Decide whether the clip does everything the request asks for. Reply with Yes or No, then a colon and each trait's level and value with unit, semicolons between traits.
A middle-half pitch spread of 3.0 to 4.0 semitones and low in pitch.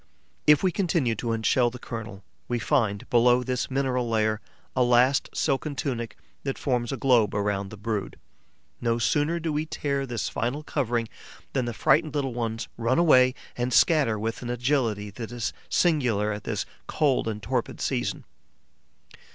Yes: average, 3.4 semitones; low, 120 Hz